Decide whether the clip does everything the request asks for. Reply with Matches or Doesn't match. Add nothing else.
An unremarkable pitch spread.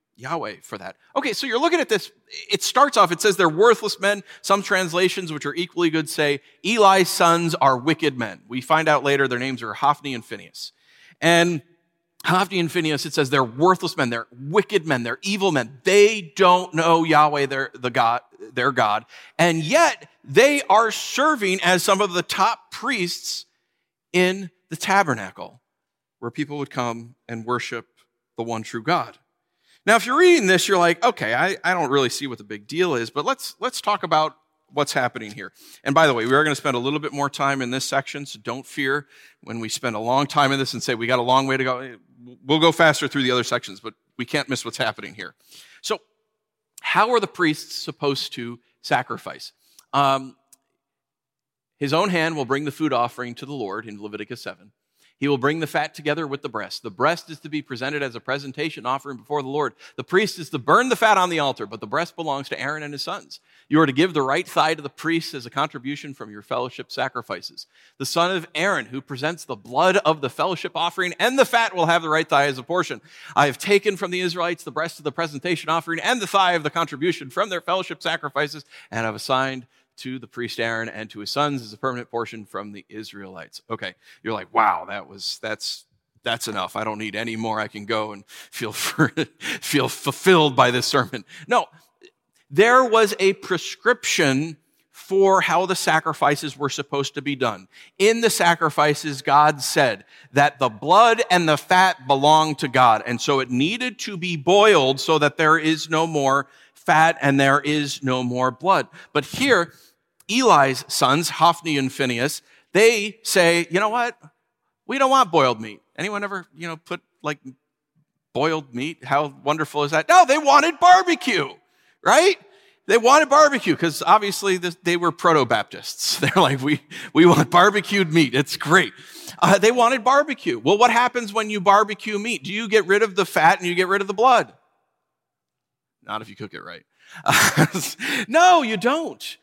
Doesn't match